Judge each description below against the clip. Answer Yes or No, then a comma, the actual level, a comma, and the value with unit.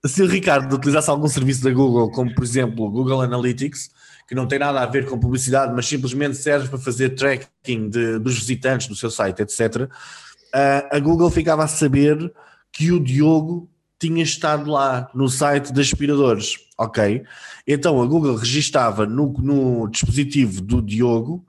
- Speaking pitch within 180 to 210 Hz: No, low, 135 Hz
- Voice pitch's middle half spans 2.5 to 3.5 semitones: Yes, average, 2.8 semitones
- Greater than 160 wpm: Yes, average, 170 wpm